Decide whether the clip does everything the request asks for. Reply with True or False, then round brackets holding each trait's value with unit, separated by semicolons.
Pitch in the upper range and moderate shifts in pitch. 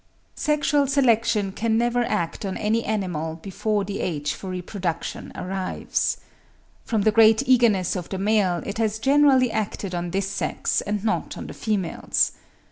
True (210 Hz; 3.5 semitones)